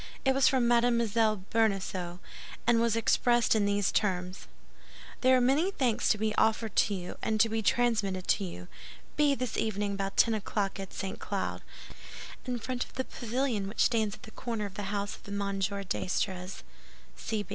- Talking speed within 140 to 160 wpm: No, average, 175 wpm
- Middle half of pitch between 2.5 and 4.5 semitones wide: Yes, average, 3.3 semitones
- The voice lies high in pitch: Yes, high, 215 Hz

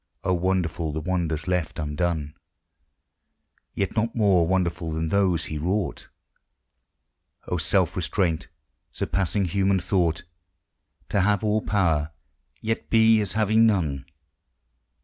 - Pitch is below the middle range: Yes, very low, 90 Hz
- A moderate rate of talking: No, slow, 115 wpm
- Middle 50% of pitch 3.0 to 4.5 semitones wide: Yes, average, 3.7 semitones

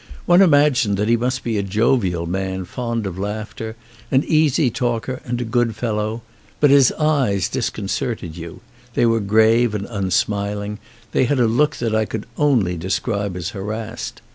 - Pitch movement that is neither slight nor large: Yes, average, 3.4 semitones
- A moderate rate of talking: Yes, average, 175 wpm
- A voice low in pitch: Yes, low, 110 Hz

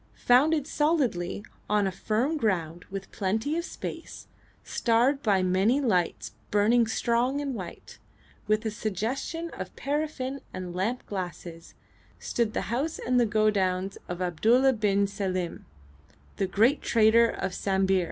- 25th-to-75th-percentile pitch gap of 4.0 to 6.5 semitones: Yes, average, 5.0 semitones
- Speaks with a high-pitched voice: Yes, high, 215 Hz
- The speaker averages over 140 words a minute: No, slow, 135 wpm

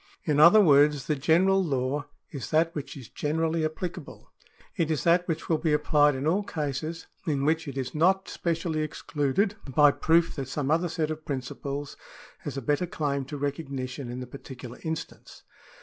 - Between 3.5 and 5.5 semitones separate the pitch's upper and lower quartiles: No, average, 2.8 semitones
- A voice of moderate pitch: Yes, medium, 150 Hz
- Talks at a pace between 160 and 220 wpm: Yes, average, 180 wpm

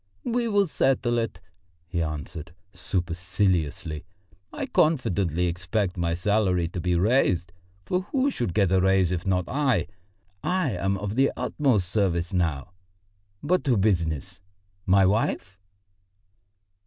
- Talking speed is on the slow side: Yes, slow, 130 wpm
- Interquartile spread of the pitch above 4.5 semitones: Yes, wide, 5.6 semitones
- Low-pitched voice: Yes, very low, 95 Hz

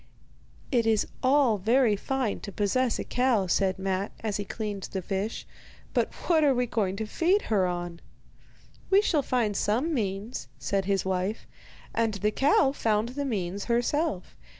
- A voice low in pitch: No, high, 215 Hz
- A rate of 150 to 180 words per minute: Yes, average, 165 wpm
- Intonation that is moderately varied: Yes, average, 4.7 semitones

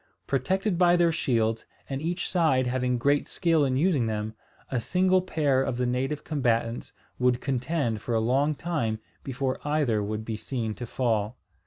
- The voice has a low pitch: Yes, low, 130 Hz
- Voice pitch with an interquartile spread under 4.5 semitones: No, average, 4.9 semitones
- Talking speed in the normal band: Yes, average, 170 wpm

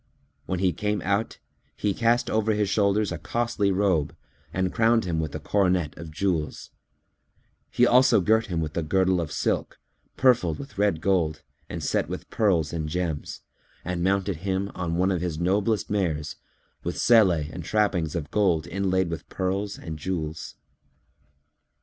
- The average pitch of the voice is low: Yes, very low, 95 Hz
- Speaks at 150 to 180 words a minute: Yes, average, 160 wpm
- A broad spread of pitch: No, average, 3.9 semitones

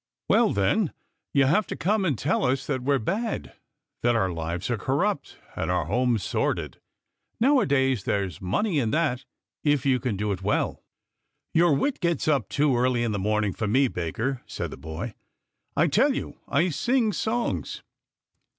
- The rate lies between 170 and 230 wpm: Yes, average, 180 wpm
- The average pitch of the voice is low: Yes, low, 130 Hz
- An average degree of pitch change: No, wide, 7.0 semitones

